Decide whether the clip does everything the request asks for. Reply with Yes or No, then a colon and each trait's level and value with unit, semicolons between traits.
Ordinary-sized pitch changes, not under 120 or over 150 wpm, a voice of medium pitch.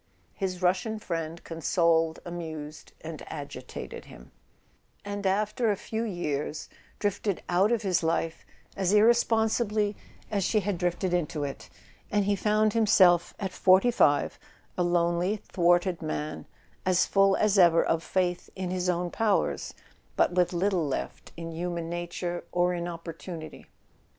Yes: average, 3.3 semitones; average, 140 wpm; medium, 180 Hz